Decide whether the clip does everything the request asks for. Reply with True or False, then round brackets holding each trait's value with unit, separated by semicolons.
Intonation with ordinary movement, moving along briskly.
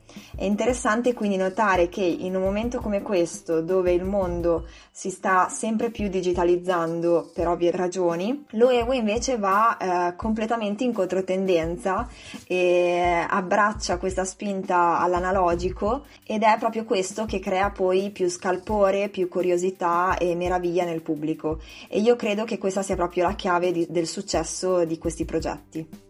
False (3.0 semitones; 145 wpm)